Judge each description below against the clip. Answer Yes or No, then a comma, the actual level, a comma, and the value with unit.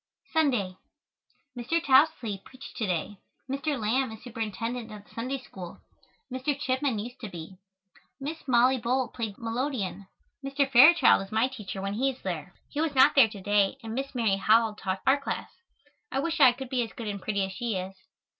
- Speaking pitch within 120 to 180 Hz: No, high, 235 Hz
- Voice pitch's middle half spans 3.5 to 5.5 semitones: Yes, average, 4.6 semitones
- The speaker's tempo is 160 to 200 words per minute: Yes, average, 190 wpm